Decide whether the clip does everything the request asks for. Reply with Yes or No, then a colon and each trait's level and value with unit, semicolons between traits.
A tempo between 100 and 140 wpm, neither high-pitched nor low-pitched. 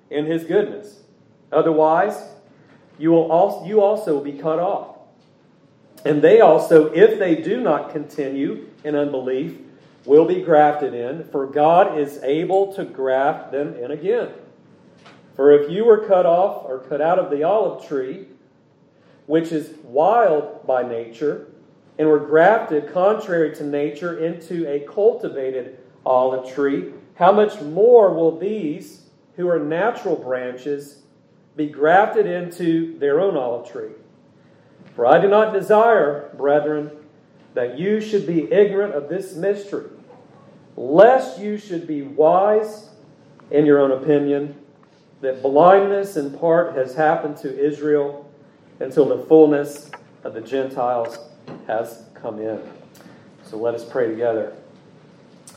Yes: slow, 135 wpm; medium, 155 Hz